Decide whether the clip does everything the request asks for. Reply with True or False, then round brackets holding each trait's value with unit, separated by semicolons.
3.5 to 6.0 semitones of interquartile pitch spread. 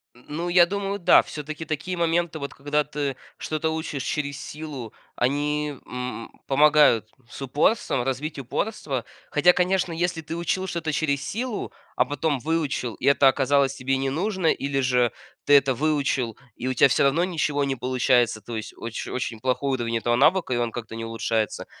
True (4.0 semitones)